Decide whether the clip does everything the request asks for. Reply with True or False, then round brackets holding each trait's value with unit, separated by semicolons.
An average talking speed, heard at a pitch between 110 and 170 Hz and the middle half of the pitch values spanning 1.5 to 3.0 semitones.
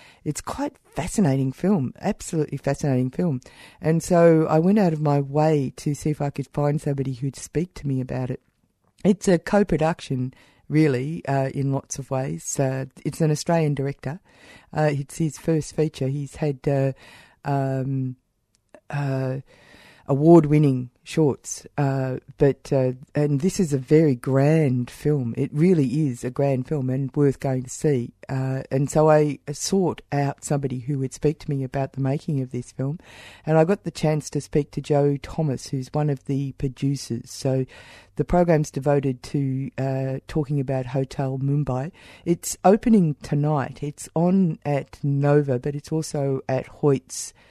True (165 wpm; 140 Hz; 2.6 semitones)